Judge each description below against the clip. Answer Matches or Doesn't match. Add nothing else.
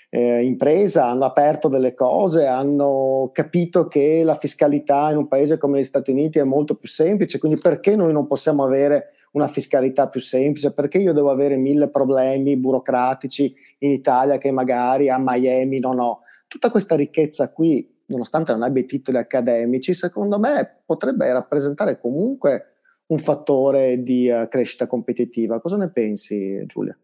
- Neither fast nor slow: Matches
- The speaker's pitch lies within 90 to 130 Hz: Doesn't match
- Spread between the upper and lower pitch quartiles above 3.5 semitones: Doesn't match